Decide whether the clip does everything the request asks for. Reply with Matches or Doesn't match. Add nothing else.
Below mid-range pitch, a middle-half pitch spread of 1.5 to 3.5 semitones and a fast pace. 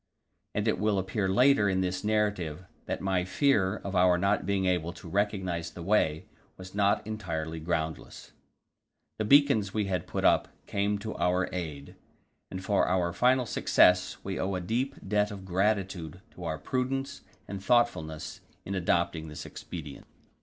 Doesn't match